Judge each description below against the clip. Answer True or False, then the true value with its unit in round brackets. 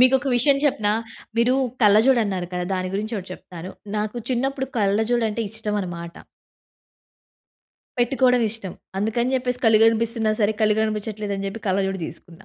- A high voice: True (215 Hz)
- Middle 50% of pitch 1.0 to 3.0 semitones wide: False (3.4 semitones)